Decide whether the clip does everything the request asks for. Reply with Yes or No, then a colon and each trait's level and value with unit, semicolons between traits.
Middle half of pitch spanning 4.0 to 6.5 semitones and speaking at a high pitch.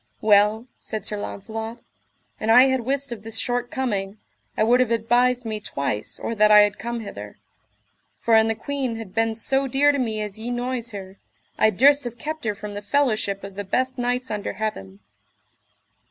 No: average, 3.0 semitones; high, 225 Hz